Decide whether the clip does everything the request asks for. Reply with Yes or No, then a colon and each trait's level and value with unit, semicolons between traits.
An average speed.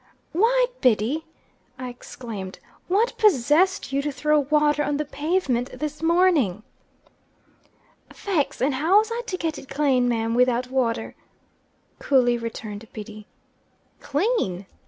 No: slow, 125 wpm